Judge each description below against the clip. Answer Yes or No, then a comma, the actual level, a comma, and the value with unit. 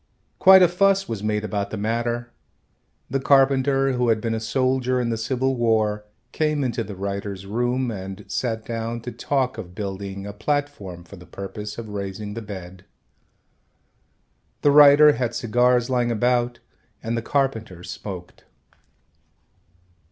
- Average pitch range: Yes, average, 4.0 semitones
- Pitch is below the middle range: Yes, low, 115 Hz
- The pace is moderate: Yes, average, 150 wpm